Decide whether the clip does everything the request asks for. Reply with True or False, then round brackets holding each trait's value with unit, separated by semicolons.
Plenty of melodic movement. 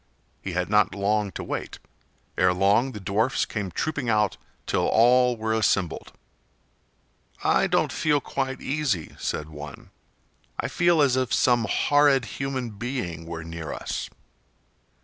True (6.1 semitones)